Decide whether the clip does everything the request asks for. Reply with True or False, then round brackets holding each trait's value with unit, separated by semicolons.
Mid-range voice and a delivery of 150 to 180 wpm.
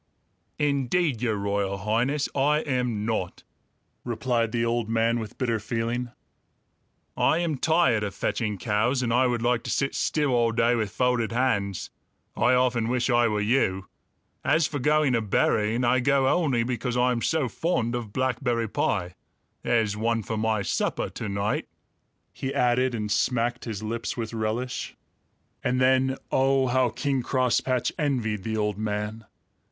False (120 Hz; 160 wpm)